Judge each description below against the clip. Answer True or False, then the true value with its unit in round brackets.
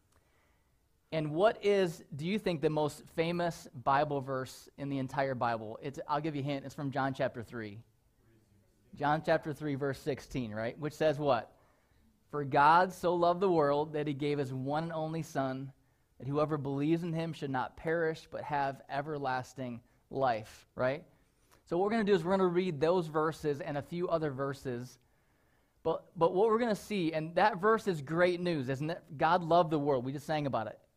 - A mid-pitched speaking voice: True (150 Hz)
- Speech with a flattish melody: False (3.7 semitones)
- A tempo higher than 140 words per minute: True (200 wpm)